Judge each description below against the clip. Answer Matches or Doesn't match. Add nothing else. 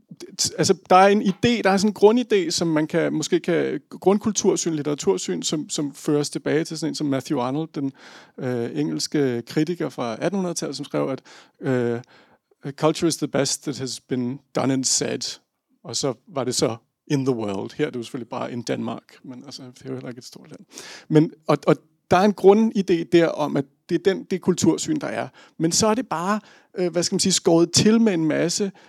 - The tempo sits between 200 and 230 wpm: Matches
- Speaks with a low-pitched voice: Doesn't match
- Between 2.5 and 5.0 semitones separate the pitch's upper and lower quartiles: Doesn't match